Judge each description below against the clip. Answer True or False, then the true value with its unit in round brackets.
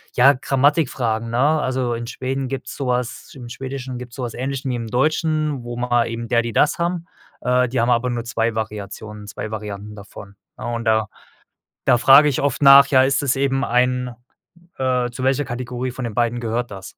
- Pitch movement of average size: False (2.3 semitones)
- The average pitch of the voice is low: True (125 Hz)